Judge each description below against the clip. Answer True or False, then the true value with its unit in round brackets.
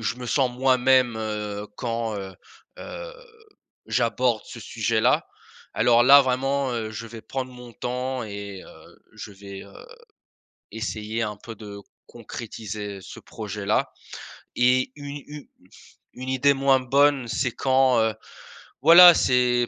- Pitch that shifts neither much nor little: True (3.3 semitones)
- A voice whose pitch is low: True (120 Hz)